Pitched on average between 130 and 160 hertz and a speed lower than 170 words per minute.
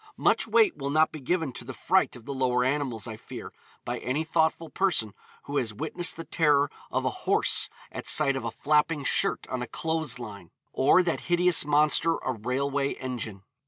No: medium, 140 Hz; average, 195 wpm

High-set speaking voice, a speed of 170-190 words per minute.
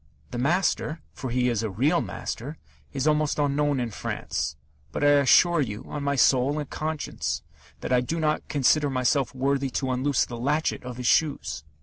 No: medium, 140 Hz; average, 185 wpm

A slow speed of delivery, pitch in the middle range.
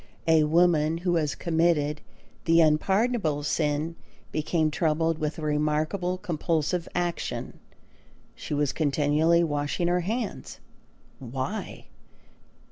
Yes: slow, 105 wpm; medium, 160 Hz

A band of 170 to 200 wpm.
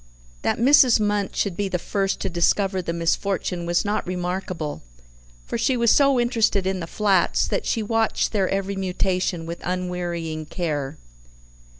No: average, 160 wpm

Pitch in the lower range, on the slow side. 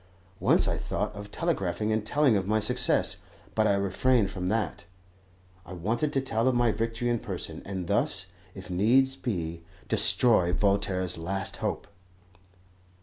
No: low, 105 Hz; average, 150 wpm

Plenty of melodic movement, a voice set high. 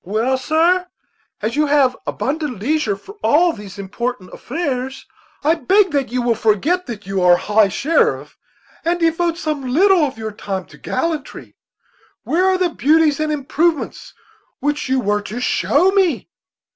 Yes: wide, 6.6 semitones; very high, 285 Hz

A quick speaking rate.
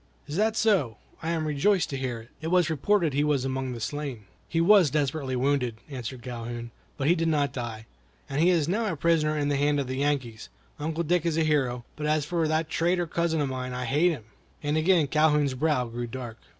Yes: fast, 225 wpm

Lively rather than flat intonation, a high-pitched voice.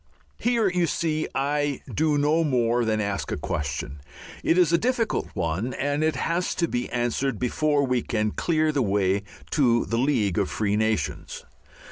No: wide, 6.4 semitones; low, 130 Hz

